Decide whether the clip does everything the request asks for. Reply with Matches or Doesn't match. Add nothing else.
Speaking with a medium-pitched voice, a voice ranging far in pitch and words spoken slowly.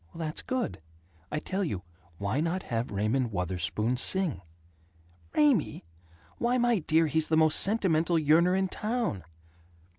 Matches